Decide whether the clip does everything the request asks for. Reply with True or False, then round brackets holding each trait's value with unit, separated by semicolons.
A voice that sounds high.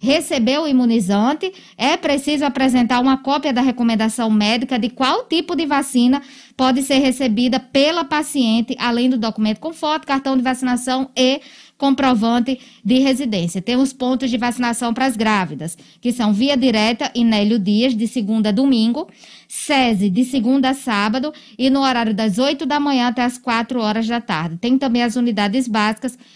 True (250 Hz)